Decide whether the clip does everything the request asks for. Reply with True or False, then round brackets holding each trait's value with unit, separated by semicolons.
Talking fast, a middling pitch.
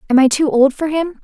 False (290 wpm; 285 Hz)